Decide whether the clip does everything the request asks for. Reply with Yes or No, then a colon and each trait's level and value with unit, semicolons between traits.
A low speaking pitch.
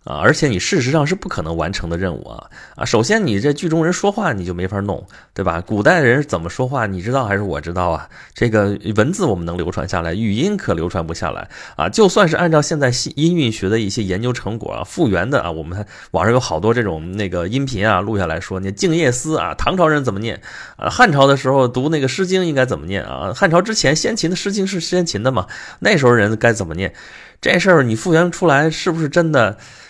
Yes: low, 115 Hz